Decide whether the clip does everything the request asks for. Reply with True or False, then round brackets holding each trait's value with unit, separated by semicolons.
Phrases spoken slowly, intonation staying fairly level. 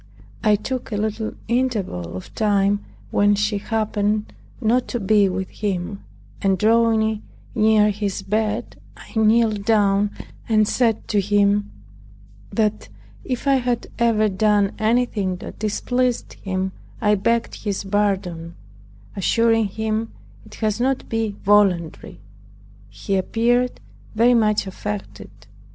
True (125 wpm; 2.0 semitones)